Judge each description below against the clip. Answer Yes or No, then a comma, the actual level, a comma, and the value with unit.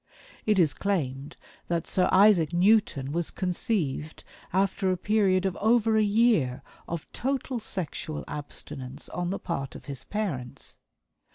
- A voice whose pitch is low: No, medium, 180 Hz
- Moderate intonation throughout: No, wide, 5.9 semitones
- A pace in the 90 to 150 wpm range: Yes, average, 140 wpm